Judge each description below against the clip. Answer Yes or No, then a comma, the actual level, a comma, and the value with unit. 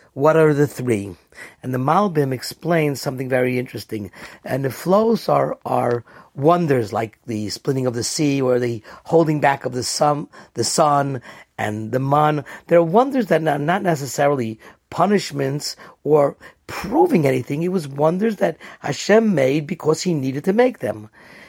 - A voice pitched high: No, medium, 140 Hz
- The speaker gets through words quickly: No, average, 160 wpm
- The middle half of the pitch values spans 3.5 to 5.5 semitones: Yes, average, 4.8 semitones